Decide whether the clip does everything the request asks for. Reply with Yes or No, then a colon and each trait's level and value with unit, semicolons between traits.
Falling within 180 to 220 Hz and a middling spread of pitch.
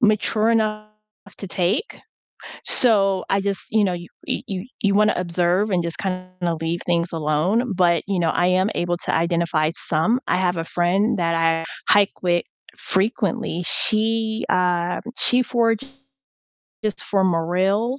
Yes: medium, 185 Hz; average, 3.6 semitones